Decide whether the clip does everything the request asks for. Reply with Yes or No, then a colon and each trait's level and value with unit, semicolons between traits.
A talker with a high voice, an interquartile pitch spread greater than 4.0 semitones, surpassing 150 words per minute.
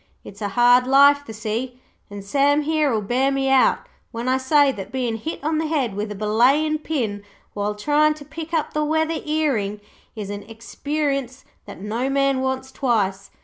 Yes: very high, 260 Hz; average, 5.3 semitones; average, 185 wpm